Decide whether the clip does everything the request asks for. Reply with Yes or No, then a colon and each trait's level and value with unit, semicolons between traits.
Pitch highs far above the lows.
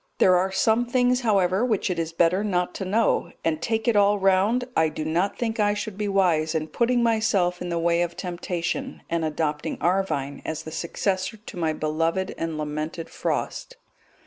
No: average, 4.3 semitones